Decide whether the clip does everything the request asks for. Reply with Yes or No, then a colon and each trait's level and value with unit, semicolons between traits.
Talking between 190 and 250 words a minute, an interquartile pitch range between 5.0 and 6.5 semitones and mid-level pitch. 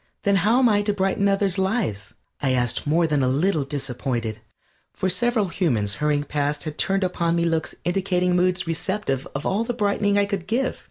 Yes: average, 195 wpm; wide, 5.4 semitones; medium, 180 Hz